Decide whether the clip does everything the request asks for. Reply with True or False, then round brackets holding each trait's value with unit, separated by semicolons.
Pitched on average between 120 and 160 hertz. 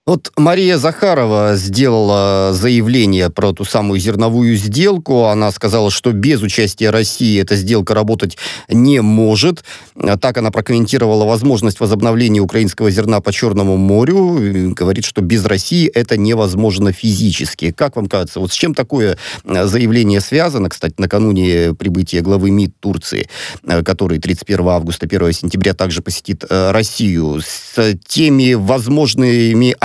False (105 Hz)